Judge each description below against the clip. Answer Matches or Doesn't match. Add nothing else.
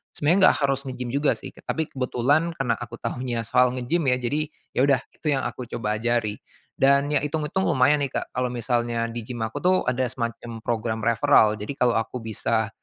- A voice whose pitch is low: Matches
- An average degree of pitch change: Matches